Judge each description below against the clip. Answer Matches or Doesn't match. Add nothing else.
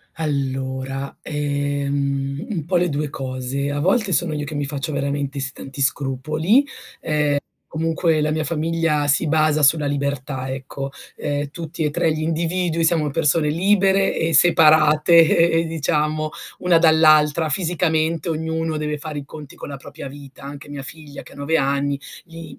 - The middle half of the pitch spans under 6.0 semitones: Matches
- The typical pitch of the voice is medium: Matches